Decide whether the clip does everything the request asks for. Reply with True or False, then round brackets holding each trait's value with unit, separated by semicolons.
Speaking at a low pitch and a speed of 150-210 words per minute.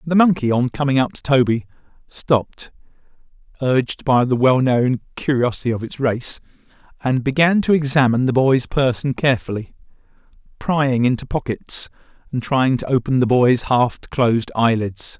False (130 Hz; 140 wpm)